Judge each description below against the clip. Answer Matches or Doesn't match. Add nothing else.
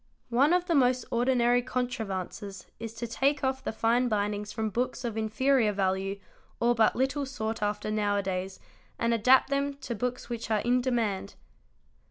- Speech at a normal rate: Matches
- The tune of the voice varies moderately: Matches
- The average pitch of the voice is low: Doesn't match